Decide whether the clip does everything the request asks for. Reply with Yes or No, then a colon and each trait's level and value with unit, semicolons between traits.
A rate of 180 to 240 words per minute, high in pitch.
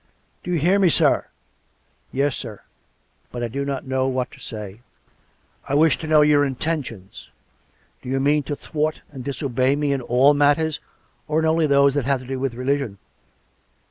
No: average, 200 wpm; medium, 140 Hz